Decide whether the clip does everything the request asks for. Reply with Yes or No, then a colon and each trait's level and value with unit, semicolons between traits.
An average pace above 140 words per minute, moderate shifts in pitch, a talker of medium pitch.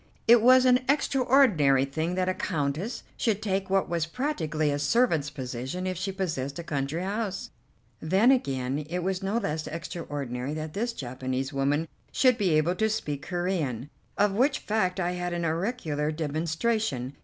No: average, 165 wpm; wide, 5.9 semitones; medium, 170 Hz